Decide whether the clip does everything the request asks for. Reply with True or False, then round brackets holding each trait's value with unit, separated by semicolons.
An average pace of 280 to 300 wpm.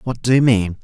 True (285 wpm)